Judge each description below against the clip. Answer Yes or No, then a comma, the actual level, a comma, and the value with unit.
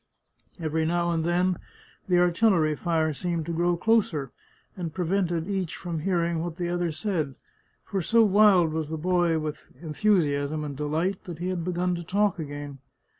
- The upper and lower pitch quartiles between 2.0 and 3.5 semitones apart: Yes, narrow, 2.5 semitones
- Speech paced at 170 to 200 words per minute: Yes, average, 175 wpm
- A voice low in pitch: No, medium, 170 Hz